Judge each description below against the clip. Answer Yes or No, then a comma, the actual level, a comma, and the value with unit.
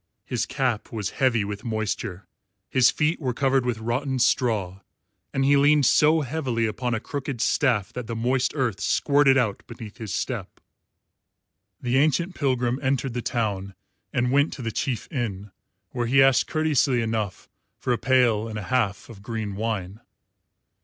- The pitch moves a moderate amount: Yes, average, 3.5 semitones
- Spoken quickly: No, average, 165 wpm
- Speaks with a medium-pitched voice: No, low, 120 Hz